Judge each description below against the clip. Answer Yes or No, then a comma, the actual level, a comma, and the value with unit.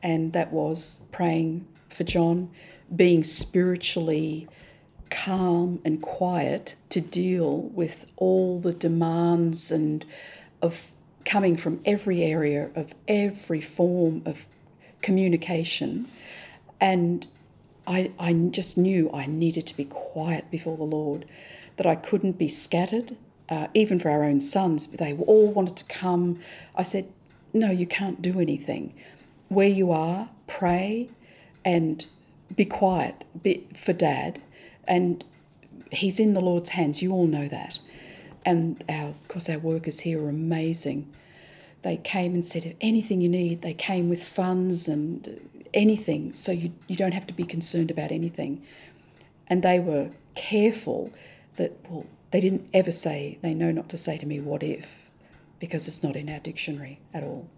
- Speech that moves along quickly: No, average, 150 wpm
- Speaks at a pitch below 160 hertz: No, medium, 170 Hz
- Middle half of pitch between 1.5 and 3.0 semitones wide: Yes, narrow, 2.6 semitones